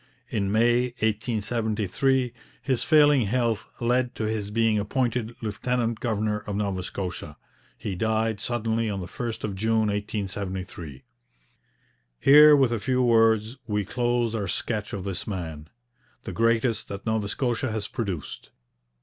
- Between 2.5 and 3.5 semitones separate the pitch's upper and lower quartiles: Yes, average, 2.9 semitones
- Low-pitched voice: Yes, low, 110 Hz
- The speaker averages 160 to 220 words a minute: No, average, 140 wpm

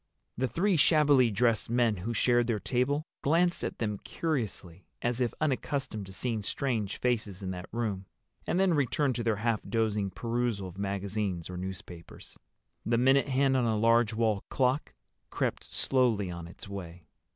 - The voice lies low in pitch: Yes, low, 115 Hz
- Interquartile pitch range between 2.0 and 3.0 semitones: No, average, 4.6 semitones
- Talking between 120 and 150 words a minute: No, average, 165 wpm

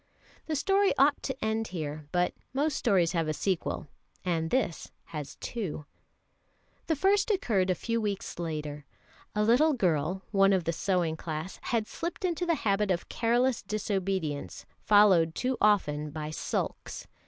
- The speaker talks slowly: No, average, 155 wpm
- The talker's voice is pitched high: Yes, high, 195 Hz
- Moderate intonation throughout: No, wide, 6.9 semitones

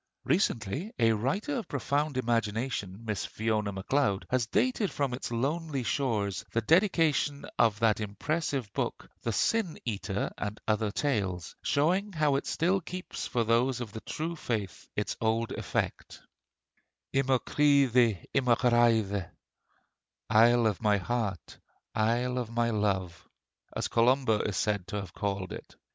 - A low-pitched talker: Yes, low, 115 Hz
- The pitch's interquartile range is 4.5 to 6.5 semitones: Yes, average, 5.0 semitones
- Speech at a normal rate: Yes, average, 145 wpm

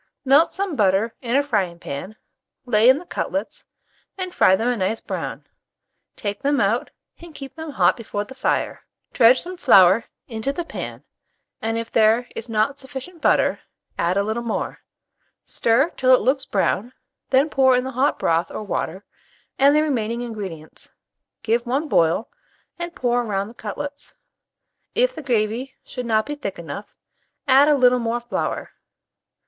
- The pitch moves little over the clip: No, average, 4.4 semitones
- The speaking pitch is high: Yes, high, 240 Hz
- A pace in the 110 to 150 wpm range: No, average, 165 wpm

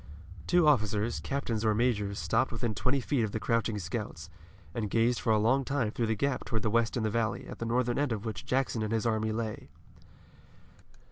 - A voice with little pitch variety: Yes, narrow, 2.3 semitones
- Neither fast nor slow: No, fast, 210 wpm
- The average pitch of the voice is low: Yes, low, 115 Hz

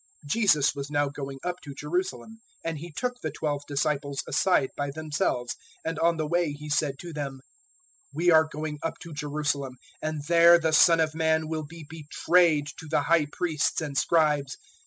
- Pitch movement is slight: Yes, narrow, 2.2 semitones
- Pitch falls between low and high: Yes, medium, 155 Hz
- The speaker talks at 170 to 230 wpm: Yes, average, 190 wpm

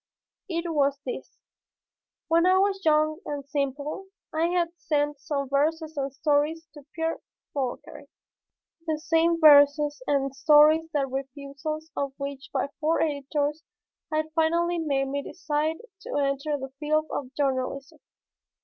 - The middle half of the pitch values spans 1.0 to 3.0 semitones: Yes, narrow, 2.5 semitones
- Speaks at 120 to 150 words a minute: Yes, slow, 135 wpm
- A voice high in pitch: Yes, very high, 295 Hz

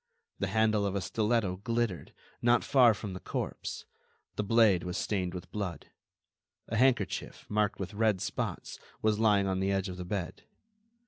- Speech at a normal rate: Yes, average, 170 wpm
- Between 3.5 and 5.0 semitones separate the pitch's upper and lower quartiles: No, average, 2.8 semitones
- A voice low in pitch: Yes, low, 105 Hz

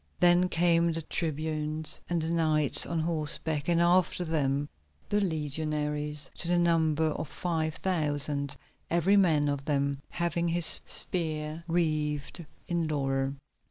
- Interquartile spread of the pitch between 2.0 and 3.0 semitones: Yes, narrow, 2.4 semitones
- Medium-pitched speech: Yes, medium, 155 Hz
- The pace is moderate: No, slow, 130 wpm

